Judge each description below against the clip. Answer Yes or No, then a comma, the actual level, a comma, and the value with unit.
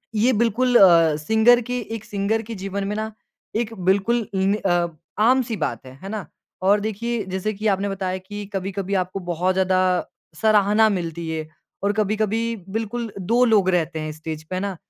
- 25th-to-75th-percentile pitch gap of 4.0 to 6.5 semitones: No, average, 3.0 semitones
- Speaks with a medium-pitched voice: No, high, 200 Hz